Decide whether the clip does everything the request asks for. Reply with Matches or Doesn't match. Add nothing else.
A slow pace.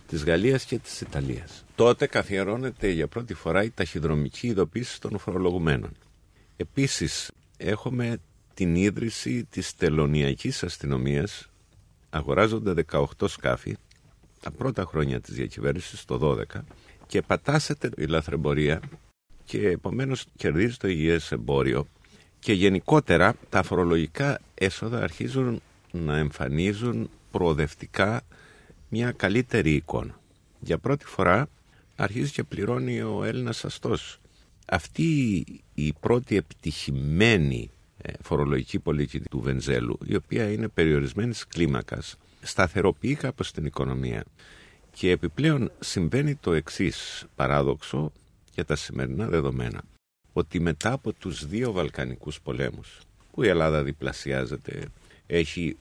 Matches